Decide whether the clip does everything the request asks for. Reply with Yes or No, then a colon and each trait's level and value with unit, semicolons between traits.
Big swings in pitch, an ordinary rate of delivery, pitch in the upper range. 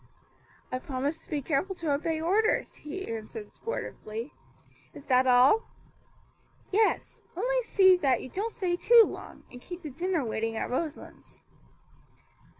Yes: wide, 6.9 semitones; average, 145 wpm; very high, 320 Hz